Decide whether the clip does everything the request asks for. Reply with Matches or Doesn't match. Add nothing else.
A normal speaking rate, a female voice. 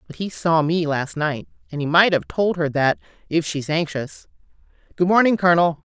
Matches